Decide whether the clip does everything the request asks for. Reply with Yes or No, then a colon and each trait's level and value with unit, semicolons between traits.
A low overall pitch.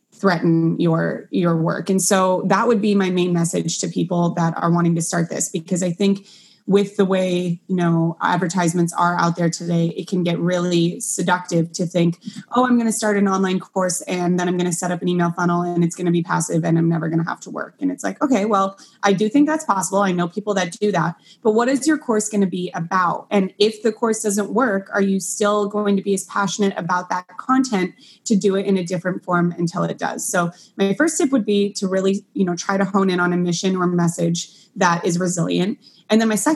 No: medium, 185 Hz